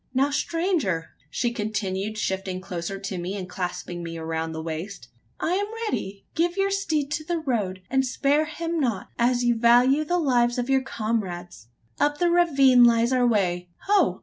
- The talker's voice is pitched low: No, high, 235 Hz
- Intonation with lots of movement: Yes, wide, 7.7 semitones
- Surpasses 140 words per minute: Yes, average, 175 wpm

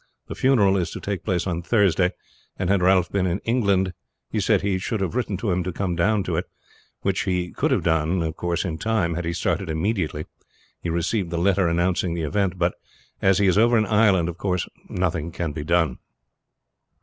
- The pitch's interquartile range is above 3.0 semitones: No, average, 2.7 semitones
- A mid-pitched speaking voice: No, very low, 90 Hz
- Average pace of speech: No, fast, 210 wpm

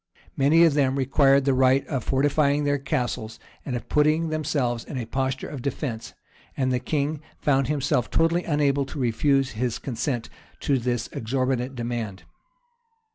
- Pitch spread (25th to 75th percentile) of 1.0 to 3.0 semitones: Yes, average, 2.7 semitones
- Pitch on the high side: No, low, 135 Hz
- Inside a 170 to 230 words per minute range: No, average, 155 wpm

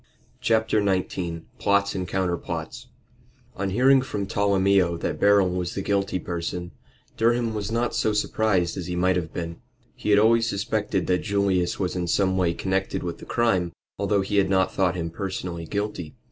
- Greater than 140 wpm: Yes, average, 175 wpm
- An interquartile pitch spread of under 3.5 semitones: Yes, narrow, 2.5 semitones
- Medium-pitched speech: No, very low, 95 Hz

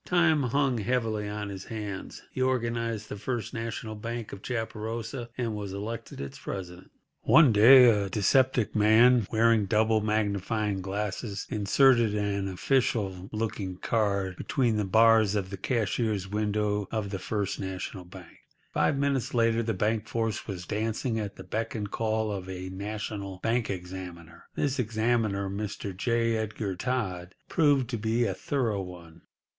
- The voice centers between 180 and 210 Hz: No, low, 110 Hz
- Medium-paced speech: Yes, average, 150 wpm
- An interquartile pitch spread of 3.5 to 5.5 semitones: No, average, 2.8 semitones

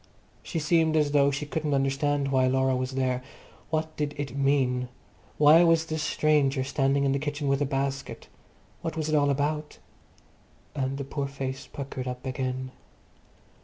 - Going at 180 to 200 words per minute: No, average, 165 wpm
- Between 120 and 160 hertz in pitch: Yes, medium, 140 Hz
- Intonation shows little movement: Yes, narrow, 2.0 semitones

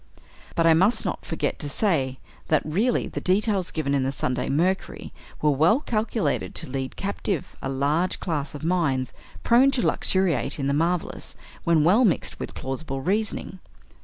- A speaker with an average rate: Yes, average, 165 wpm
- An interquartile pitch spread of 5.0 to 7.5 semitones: Yes, wide, 5.6 semitones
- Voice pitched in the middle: Yes, medium, 165 Hz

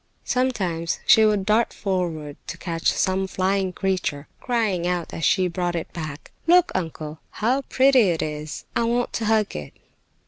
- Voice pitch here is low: No, medium, 185 Hz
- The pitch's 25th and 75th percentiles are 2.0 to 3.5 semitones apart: No, average, 4.7 semitones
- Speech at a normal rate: Yes, average, 165 wpm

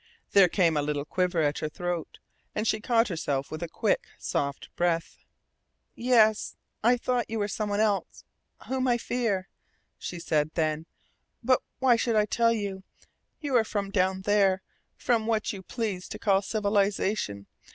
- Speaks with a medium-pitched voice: No, high, 200 Hz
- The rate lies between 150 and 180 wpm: Yes, average, 165 wpm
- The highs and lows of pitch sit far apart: No, average, 4.5 semitones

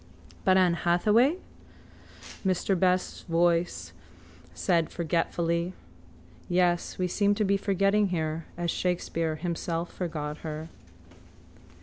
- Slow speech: Yes, slow, 105 wpm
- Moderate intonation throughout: No, narrow, 2.1 semitones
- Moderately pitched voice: Yes, medium, 175 Hz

